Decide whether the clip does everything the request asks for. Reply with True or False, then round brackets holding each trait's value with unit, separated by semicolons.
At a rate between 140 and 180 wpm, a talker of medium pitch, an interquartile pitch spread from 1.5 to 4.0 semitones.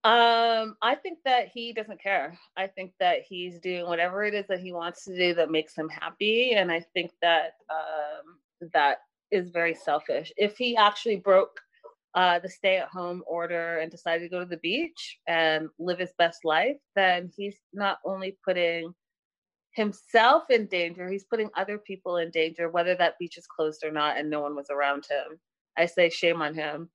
False (195 wpm; 180 Hz; 3.5 semitones)